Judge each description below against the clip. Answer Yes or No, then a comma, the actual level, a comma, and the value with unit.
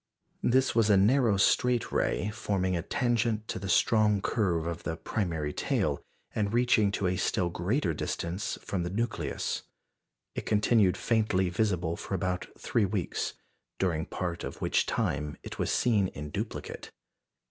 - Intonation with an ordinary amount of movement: Yes, average, 4.0 semitones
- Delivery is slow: No, average, 155 wpm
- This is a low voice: Yes, low, 100 Hz